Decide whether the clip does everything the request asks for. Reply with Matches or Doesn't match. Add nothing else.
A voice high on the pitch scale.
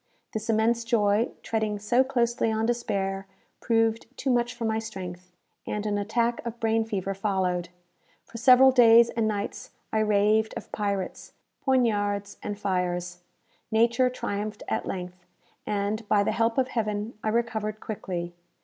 Matches